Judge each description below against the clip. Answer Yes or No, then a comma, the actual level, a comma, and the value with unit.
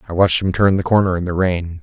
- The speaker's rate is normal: No, fast, 295 wpm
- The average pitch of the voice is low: Yes, very low, 90 Hz